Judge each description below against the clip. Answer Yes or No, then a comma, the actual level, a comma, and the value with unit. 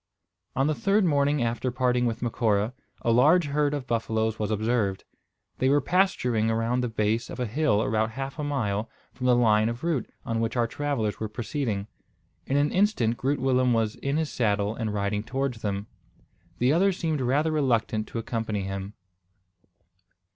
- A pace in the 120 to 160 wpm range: No, average, 175 wpm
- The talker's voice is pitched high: No, low, 120 Hz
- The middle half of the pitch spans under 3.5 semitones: No, average, 4.3 semitones